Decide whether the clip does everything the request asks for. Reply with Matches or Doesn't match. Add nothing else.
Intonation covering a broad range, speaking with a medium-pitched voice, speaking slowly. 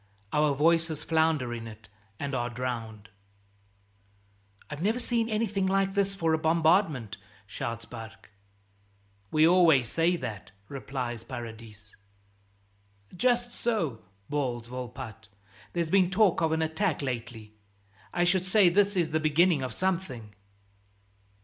Matches